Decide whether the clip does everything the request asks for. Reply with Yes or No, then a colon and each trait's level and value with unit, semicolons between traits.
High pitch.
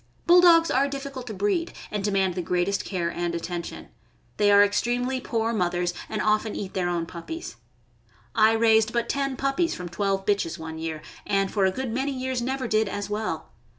Yes: high, 210 Hz